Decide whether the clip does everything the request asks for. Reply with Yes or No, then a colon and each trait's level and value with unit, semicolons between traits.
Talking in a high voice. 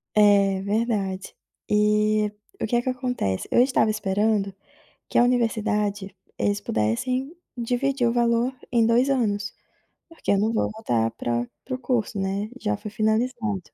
Yes: high, 215 Hz